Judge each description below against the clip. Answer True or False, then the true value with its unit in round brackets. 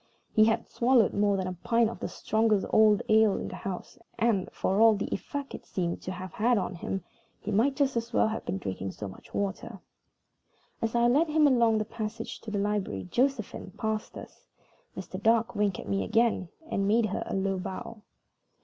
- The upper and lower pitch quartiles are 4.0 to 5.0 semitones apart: False (3.2 semitones)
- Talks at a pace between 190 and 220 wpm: True (205 wpm)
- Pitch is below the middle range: False (215 Hz)